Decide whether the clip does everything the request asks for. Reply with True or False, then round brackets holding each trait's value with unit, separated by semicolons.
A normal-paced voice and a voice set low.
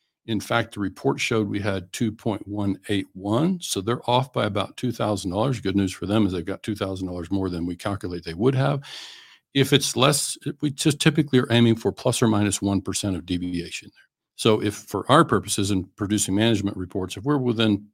True (190 wpm; 105 Hz)